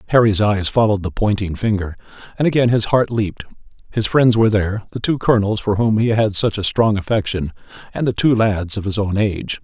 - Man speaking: Yes, male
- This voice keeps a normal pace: No, fast, 210 wpm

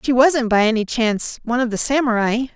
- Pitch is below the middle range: No, high, 240 Hz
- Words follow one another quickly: Yes, fast, 210 wpm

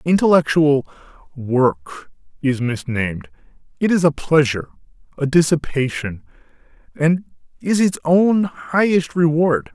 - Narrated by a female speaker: No, male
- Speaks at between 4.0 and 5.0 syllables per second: Yes, 4.2 syllables/s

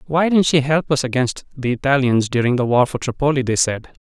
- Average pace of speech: No, fast, 225 wpm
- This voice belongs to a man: Yes, male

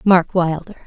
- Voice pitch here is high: No, medium, 180 Hz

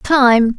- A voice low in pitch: No, very high, 250 Hz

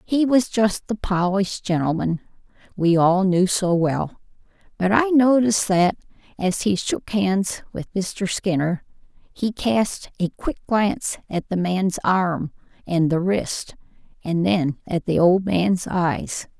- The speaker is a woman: Yes, female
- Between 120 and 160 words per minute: Yes, average, 150 wpm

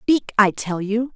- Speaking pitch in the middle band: No, high, 220 Hz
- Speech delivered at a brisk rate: Yes, fast, 210 wpm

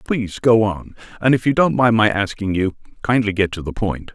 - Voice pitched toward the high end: No, low, 105 Hz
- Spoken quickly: Yes, fast, 230 wpm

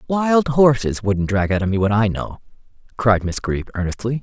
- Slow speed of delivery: No, average, 200 wpm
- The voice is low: Yes, low, 115 Hz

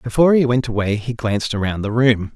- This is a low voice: Yes, low, 115 Hz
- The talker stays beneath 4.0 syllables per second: No, 6.1 syllables/s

